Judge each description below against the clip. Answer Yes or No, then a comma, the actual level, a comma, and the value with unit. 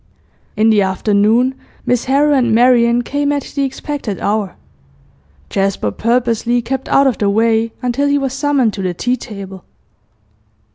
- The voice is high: Yes, high, 235 Hz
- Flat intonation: No, average, 4.1 semitones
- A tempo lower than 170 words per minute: Yes, average, 150 wpm